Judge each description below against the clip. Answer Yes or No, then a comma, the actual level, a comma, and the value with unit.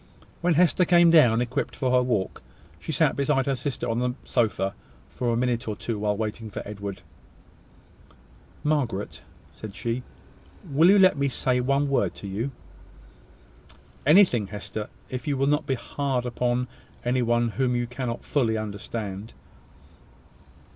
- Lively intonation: No, average, 3.8 semitones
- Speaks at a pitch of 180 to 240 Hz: No, low, 125 Hz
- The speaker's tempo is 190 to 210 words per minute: No, average, 155 wpm